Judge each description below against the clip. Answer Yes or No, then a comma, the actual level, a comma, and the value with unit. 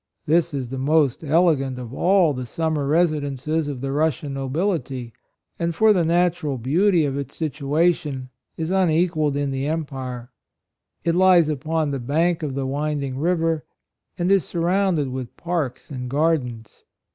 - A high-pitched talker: No, medium, 150 Hz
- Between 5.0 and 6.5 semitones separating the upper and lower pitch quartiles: No, average, 3.8 semitones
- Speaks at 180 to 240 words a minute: No, average, 155 wpm